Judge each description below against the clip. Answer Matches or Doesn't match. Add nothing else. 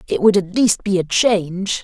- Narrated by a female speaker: Doesn't match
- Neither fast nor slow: Doesn't match